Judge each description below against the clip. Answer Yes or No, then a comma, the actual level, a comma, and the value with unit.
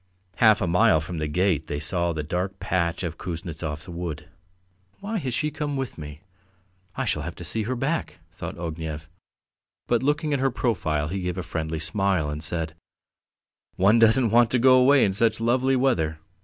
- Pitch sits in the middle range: No, very low, 90 Hz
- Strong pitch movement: Yes, wide, 7.0 semitones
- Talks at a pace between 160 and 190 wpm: Yes, average, 185 wpm